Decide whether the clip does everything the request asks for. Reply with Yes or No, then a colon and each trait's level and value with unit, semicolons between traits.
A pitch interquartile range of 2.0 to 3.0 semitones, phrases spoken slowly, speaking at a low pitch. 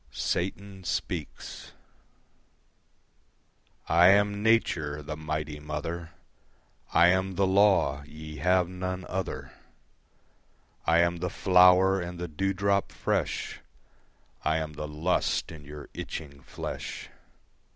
No: average, 3.6 semitones; slow, 110 wpm; very low, 85 Hz